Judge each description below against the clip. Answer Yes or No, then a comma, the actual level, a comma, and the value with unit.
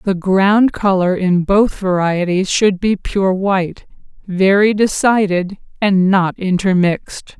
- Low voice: No, high, 190 Hz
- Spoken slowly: Yes, slow, 120 wpm